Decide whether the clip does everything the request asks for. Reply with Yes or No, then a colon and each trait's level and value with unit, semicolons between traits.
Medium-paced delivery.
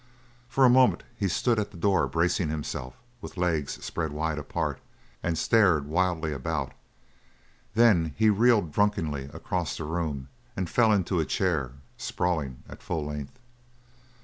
Yes: average, 150 wpm